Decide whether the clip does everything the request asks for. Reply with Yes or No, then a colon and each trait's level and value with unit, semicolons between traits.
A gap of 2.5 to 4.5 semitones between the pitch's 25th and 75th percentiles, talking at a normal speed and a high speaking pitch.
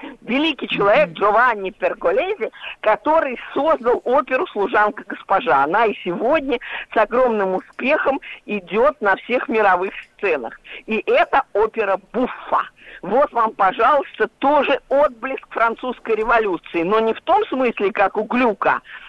No: wide, 5.6 semitones; average, 125 wpm; high, 235 Hz